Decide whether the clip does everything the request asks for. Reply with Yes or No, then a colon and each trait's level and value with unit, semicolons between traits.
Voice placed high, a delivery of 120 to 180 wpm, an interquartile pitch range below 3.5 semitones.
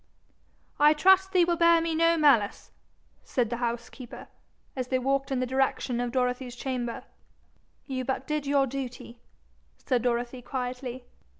Yes: very high, 260 Hz; average, 145 wpm; average, 3.0 semitones